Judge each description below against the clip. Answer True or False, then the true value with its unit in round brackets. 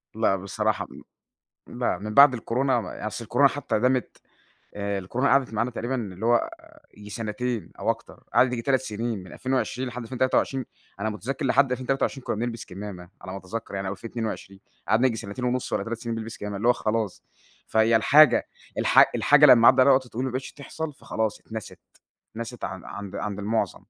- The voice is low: True (115 Hz)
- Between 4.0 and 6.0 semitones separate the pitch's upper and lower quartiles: False (3.6 semitones)